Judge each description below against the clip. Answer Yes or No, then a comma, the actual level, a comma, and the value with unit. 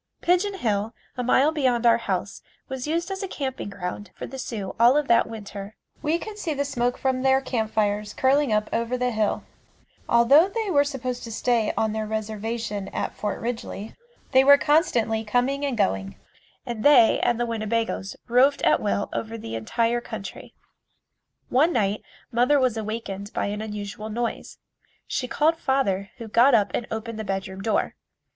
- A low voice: No, high, 235 Hz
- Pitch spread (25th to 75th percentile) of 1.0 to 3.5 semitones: No, average, 3.9 semitones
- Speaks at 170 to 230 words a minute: Yes, average, 175 wpm